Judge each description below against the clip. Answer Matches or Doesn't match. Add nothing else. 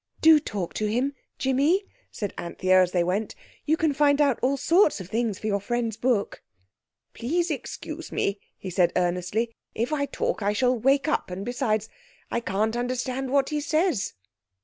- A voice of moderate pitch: Doesn't match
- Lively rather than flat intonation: Matches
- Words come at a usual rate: Matches